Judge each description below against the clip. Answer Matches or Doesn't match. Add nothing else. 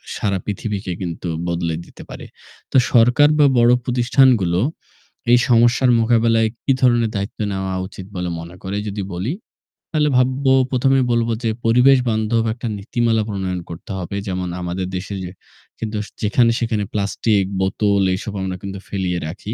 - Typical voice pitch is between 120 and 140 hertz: Doesn't match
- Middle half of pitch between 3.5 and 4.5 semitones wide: Matches